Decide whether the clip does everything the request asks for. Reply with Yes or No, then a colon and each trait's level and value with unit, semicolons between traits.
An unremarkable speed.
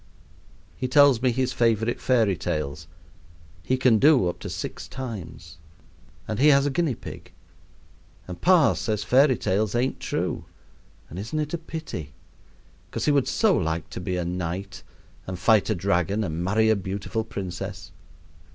Yes: average, 160 wpm